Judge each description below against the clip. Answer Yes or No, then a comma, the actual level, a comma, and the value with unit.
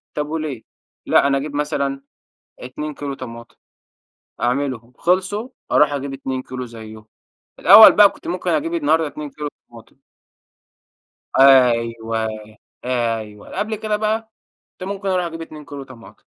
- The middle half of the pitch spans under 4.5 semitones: No, average, 5.0 semitones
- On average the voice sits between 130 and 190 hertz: Yes, medium, 140 Hz